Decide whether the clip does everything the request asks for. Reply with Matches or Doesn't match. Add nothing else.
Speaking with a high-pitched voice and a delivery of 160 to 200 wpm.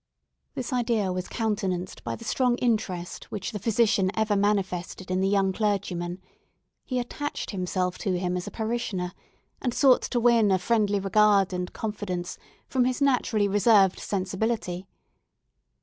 Doesn't match